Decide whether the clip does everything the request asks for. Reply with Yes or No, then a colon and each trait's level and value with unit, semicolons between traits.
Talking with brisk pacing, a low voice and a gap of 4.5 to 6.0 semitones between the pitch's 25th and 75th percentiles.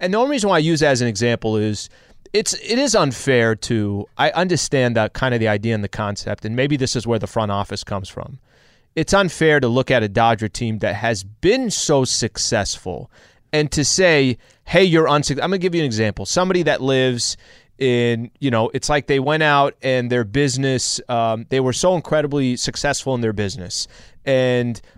Yes: fast, 210 wpm; low, 130 Hz; average, 4.8 semitones